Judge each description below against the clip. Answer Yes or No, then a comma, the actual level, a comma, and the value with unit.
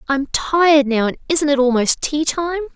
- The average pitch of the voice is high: Yes, very high, 290 Hz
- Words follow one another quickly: No, average, 195 wpm